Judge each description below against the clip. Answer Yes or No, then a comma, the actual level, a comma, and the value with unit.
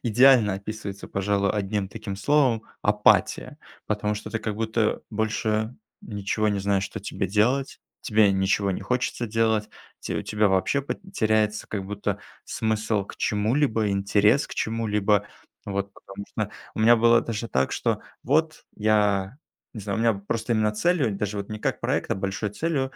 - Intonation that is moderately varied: No, narrow, 2.0 semitones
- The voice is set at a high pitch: No, low, 105 Hz